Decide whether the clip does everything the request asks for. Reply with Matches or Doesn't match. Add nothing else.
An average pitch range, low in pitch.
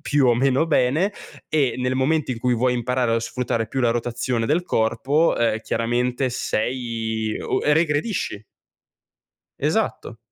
Matches